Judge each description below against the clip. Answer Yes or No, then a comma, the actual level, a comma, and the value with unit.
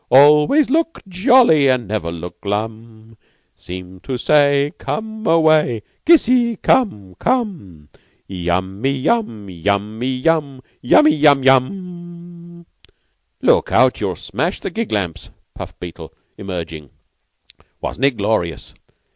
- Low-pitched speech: Yes, low, 130 Hz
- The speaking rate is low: Yes, slow, 110 wpm